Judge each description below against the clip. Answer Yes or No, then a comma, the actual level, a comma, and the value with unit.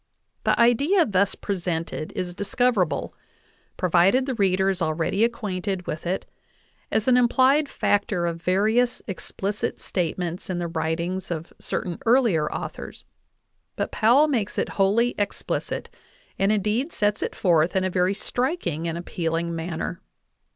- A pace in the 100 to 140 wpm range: Yes, slow, 135 wpm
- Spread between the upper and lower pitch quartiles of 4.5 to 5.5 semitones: Yes, average, 4.8 semitones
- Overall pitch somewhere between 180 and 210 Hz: Yes, high, 190 Hz